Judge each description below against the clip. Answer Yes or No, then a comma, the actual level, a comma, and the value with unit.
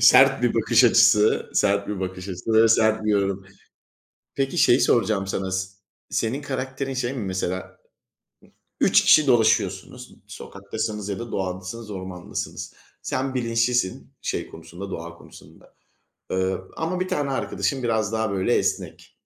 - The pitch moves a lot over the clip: No, average, 4.4 semitones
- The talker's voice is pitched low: Yes, low, 110 Hz